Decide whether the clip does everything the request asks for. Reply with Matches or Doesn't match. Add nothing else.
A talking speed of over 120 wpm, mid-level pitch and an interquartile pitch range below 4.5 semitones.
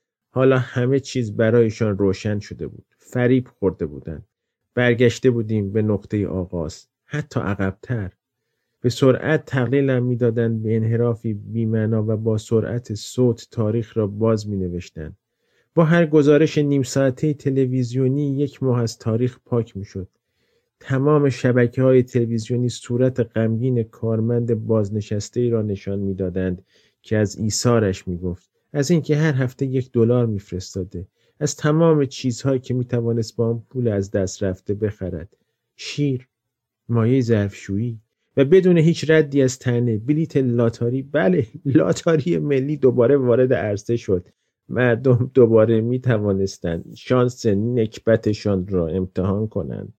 Doesn't match